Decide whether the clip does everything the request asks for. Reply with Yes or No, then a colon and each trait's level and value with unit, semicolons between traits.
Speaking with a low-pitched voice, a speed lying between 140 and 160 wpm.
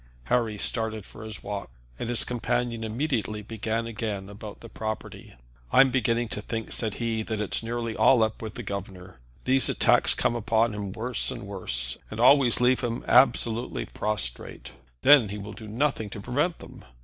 No: low, 110 Hz; average, 175 wpm